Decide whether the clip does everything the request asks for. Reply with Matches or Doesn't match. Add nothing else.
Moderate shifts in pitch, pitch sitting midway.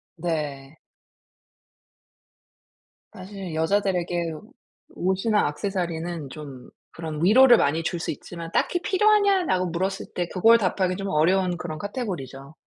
Matches